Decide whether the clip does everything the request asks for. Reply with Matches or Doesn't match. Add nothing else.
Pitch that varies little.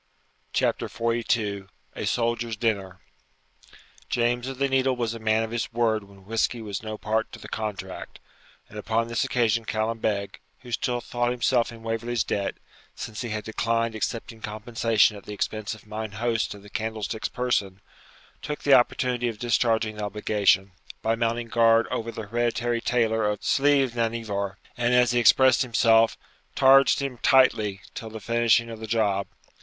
Matches